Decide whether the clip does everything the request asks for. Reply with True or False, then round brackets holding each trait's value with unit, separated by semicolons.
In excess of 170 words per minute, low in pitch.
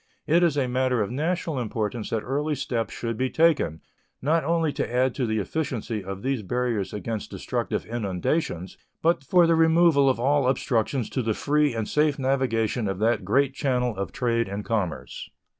True (180 wpm; 125 Hz)